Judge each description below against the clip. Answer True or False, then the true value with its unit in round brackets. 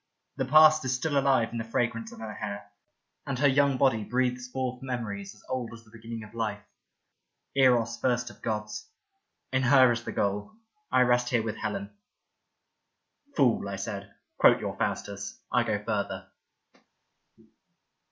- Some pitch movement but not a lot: True (3.3 semitones)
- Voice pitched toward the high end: False (120 Hz)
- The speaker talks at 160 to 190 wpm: True (170 wpm)